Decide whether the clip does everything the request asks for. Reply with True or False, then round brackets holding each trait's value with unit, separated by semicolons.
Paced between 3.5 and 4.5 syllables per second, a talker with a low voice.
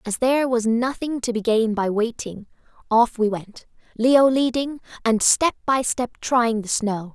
False (4.4 syllables/s; 235 Hz)